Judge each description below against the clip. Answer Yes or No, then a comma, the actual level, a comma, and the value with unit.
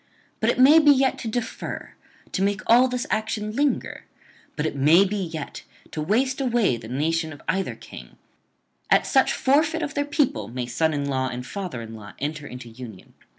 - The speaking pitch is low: No, medium, 185 Hz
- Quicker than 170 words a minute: Yes, average, 195 wpm